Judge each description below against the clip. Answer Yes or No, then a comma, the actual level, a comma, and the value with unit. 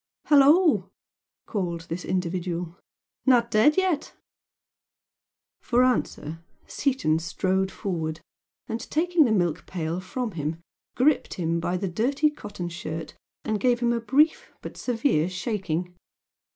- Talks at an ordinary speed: No, slow, 125 wpm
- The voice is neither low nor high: No, high, 195 Hz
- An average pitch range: No, wide, 6.8 semitones